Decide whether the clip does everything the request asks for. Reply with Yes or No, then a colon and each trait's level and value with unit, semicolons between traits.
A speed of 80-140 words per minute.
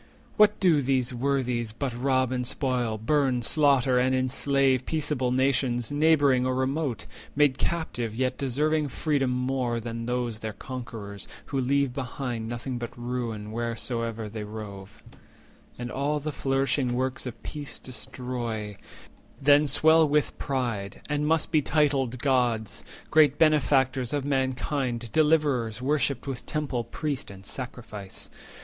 Yes: slow, 135 wpm